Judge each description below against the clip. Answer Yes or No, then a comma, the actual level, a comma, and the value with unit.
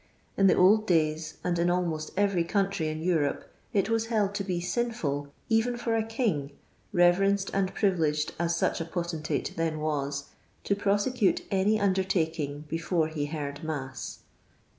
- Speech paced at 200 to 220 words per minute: No, average, 155 wpm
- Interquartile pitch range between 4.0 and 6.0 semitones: Yes, average, 4.4 semitones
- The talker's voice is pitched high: No, medium, 175 Hz